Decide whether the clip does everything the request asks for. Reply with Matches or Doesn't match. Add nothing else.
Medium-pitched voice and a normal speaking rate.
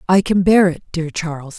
Doesn't match